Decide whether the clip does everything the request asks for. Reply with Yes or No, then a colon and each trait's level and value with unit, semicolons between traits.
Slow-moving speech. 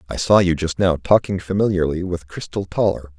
No: average, 190 wpm